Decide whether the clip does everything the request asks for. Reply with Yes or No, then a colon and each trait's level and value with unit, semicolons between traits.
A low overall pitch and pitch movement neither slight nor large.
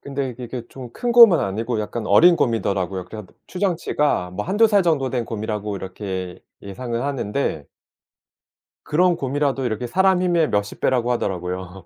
No: low, 120 Hz; wide, 6.9 semitones